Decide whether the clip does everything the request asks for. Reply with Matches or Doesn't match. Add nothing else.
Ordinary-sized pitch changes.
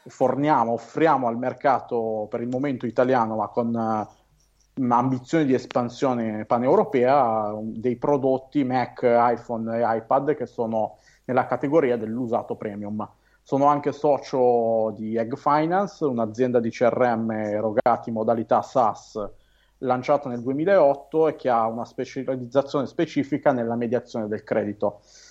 Matches